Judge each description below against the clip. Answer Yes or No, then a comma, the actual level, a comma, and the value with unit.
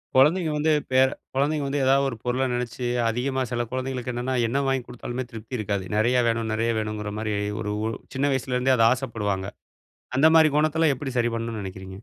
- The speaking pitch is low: Yes, low, 125 Hz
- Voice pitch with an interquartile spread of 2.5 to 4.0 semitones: Yes, average, 3.1 semitones